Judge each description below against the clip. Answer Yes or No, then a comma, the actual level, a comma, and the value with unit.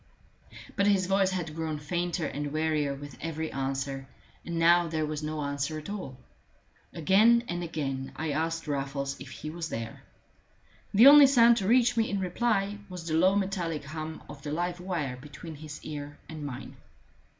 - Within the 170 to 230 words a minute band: Yes, average, 175 wpm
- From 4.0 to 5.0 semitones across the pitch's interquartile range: Yes, average, 4.3 semitones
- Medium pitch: Yes, medium, 160 Hz